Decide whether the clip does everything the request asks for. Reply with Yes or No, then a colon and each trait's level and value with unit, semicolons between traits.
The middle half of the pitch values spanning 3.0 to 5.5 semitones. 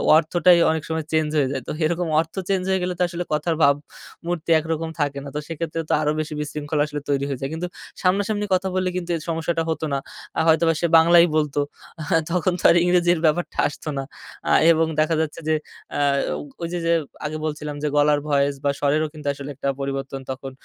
No: narrow, 2.6 semitones